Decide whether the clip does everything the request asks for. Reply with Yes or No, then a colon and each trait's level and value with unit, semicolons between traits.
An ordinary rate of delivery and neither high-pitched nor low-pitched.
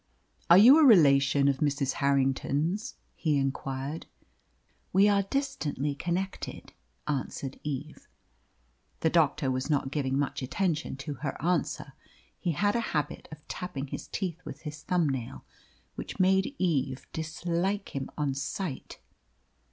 No: slow, 130 wpm; medium, 150 Hz